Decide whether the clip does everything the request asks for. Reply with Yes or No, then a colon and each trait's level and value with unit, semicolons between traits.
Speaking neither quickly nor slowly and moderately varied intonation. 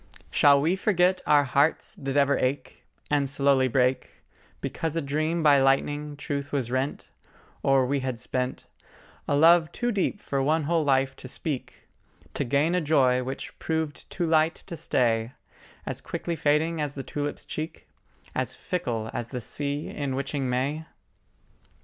Yes: average, 160 wpm; average, 3.0 semitones